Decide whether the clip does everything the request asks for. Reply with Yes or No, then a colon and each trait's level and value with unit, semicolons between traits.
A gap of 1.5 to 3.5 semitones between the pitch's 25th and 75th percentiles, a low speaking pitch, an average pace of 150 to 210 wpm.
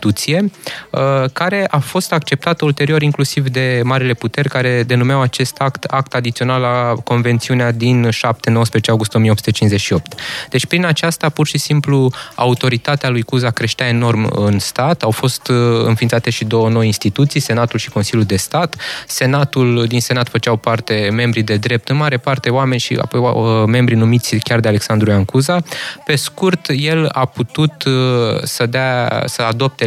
Yes: average, 3.1 semitones; low, 125 Hz; average, 155 wpm